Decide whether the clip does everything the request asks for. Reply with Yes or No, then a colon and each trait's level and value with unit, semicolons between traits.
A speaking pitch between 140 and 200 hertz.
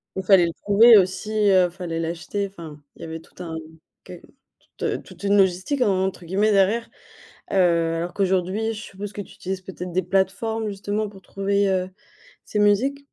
Yes: high, 190 Hz